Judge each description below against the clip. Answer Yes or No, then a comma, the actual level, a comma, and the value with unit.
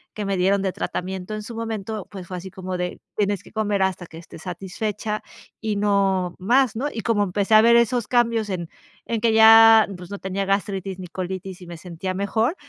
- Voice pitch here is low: No, high, 200 Hz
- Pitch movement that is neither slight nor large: Yes, average, 3.0 semitones